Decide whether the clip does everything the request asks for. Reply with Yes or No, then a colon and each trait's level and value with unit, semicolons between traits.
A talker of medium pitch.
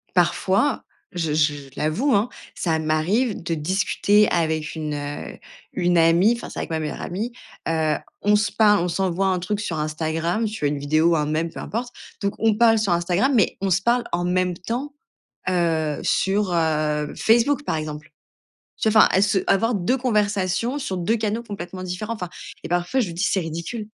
Yes: medium, 180 Hz